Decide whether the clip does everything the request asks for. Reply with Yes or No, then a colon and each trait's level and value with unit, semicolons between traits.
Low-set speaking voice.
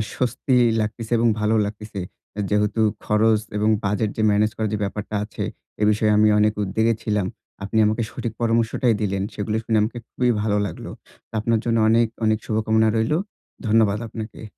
Yes: low, 110 Hz